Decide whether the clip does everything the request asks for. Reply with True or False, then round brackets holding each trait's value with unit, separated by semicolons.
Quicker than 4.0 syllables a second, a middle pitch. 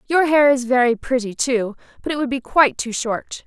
False (5.3 syllables/s; 255 Hz)